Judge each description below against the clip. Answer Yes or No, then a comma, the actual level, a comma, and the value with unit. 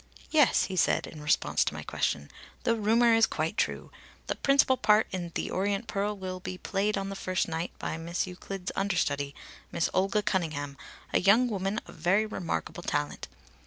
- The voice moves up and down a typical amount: Yes, average, 3.6 semitones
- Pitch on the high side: Yes, high, 195 Hz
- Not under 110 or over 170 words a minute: No, average, 180 wpm